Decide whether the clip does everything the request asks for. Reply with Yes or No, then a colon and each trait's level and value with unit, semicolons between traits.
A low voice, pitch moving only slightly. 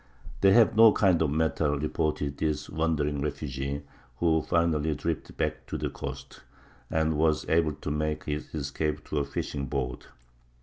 Yes: very low, 75 Hz; narrow, 2.0 semitones